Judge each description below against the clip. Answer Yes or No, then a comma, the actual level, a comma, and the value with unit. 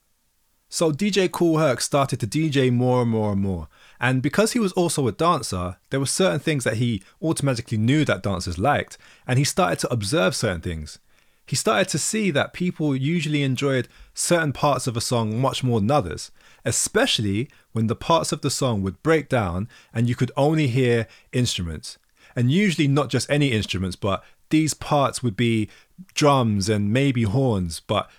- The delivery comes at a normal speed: Yes, average, 185 wpm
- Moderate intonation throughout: No, wide, 5.8 semitones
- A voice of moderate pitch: No, low, 130 Hz